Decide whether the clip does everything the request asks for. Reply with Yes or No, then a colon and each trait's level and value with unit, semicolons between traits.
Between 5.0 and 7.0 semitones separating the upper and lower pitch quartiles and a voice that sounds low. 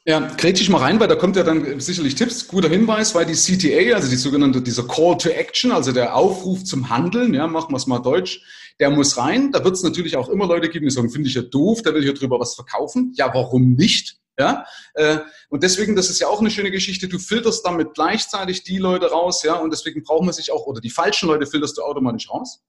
No: average, 5.3 semitones; medium, 165 Hz